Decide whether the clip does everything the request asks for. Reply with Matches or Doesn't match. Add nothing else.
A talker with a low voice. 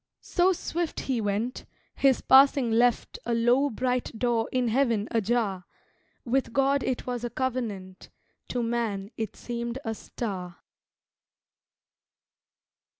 Doesn't match